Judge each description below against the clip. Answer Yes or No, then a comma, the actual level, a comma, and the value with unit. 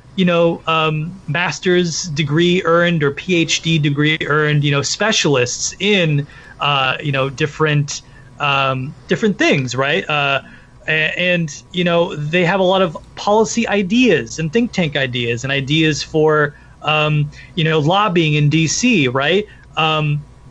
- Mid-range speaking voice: Yes, medium, 155 Hz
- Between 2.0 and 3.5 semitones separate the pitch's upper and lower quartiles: No, average, 3.9 semitones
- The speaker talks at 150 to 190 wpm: No, average, 140 wpm